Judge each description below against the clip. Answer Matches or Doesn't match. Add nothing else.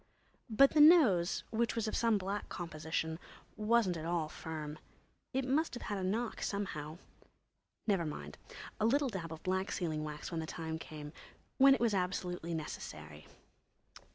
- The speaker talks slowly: Doesn't match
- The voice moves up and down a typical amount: Doesn't match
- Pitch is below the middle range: Doesn't match